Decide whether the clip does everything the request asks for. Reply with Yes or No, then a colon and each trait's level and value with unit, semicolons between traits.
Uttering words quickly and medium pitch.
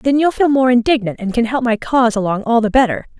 No: fast, 265 wpm; high, 240 Hz